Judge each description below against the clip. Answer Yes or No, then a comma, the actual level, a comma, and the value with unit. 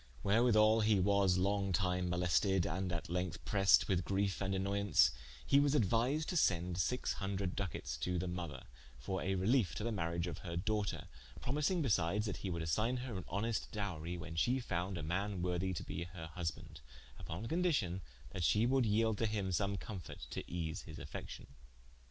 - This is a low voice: Yes, very low, 95 Hz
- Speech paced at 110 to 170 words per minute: No, average, 185 wpm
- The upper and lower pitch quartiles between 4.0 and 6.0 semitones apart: No, average, 3.6 semitones